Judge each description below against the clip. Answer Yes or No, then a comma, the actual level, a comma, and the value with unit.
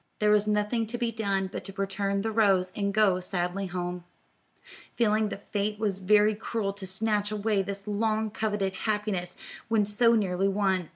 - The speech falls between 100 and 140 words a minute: No, average, 175 wpm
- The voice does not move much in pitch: Yes, narrow, 1.9 semitones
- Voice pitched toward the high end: Yes, high, 205 Hz